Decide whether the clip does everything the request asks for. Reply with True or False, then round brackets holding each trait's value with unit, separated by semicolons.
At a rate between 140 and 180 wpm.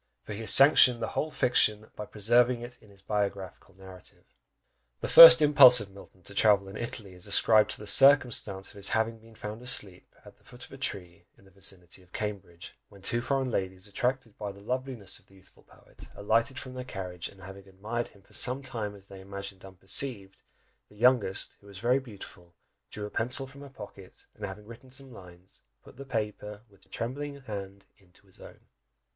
False (205 wpm)